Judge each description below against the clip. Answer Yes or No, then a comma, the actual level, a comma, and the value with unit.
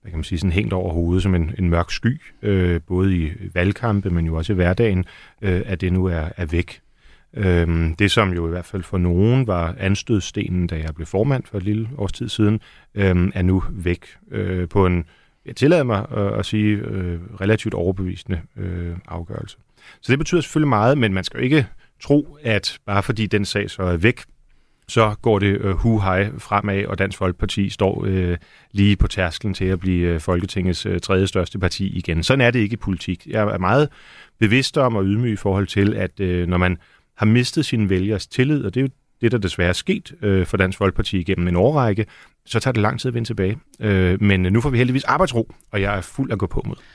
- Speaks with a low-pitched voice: Yes, low, 100 Hz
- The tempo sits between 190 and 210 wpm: No, average, 220 wpm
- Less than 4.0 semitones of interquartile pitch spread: Yes, average, 3.5 semitones